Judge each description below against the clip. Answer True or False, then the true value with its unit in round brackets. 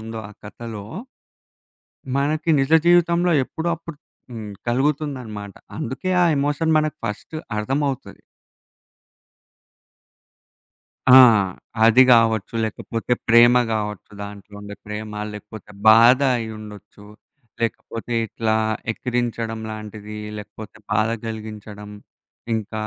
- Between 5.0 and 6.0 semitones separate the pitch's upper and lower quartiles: False (3.6 semitones)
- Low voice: True (115 Hz)